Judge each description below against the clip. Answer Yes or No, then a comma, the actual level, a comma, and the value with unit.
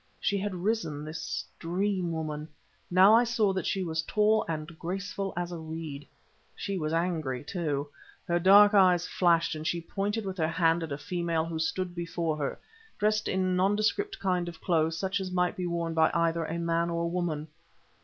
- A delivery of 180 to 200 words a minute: Yes, average, 190 wpm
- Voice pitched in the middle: Yes, medium, 175 Hz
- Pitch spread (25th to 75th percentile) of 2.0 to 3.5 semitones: Yes, average, 2.9 semitones